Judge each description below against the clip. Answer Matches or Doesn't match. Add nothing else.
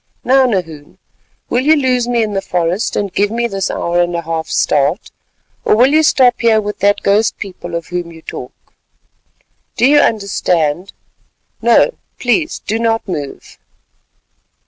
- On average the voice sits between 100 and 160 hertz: Doesn't match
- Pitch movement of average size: Doesn't match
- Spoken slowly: Doesn't match